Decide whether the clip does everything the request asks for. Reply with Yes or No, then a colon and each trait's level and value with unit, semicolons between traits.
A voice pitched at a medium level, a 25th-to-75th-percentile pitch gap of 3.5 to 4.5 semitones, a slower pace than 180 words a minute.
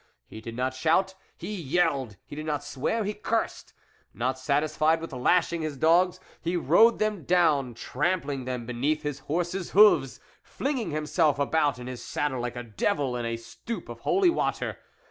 No: medium, 150 Hz; wide, 5.6 semitones; average, 170 wpm